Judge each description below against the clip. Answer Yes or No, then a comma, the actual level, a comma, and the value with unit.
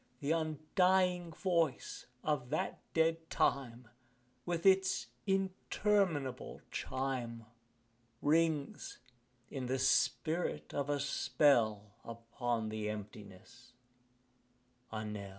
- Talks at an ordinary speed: No, slow, 90 wpm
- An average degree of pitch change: No, wide, 6.1 semitones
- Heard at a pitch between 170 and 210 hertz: No, medium, 140 Hz